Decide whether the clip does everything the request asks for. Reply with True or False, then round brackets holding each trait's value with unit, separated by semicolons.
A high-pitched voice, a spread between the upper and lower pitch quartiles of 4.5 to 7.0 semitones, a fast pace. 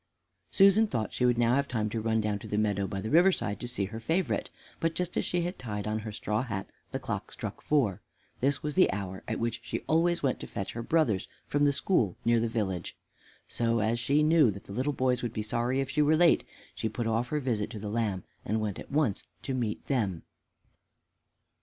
False (115 Hz; 5.2 semitones; 235 wpm)